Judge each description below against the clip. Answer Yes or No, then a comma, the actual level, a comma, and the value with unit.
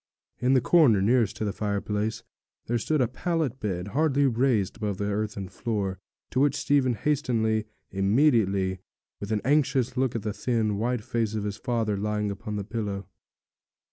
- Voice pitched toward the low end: Yes, low, 110 Hz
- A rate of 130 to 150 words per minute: No, average, 170 wpm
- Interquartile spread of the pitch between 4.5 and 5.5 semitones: No, average, 3.8 semitones